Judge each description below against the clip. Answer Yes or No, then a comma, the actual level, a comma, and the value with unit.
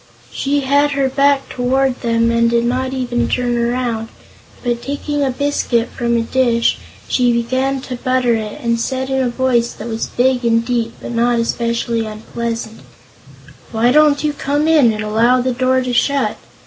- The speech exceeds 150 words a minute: Yes, average, 175 wpm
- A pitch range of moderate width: No, narrow, 2.2 semitones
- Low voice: No, high, 245 Hz